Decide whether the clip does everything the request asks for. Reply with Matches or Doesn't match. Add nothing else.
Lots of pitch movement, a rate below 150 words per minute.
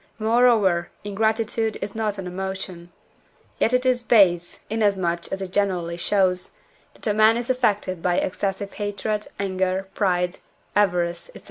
Doesn't match